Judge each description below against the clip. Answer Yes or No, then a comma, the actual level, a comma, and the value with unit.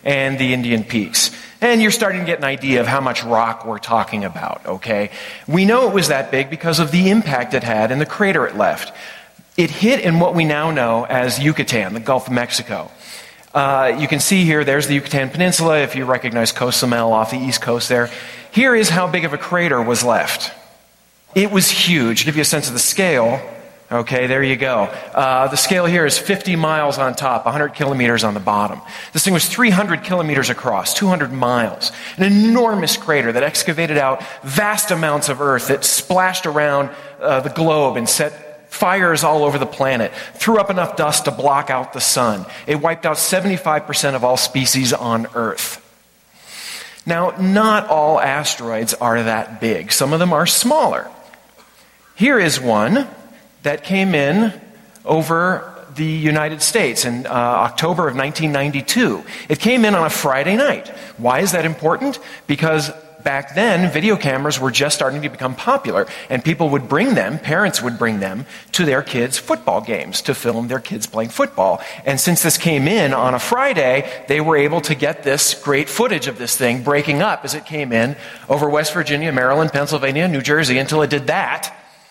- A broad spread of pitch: No, average, 4.9 semitones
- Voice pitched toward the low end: No, medium, 145 Hz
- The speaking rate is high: No, average, 190 wpm